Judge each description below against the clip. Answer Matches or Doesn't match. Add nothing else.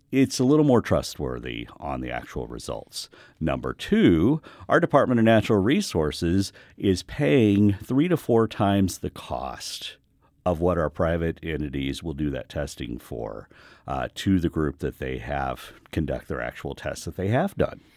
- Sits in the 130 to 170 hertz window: Doesn't match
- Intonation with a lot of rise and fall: Matches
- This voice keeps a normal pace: Matches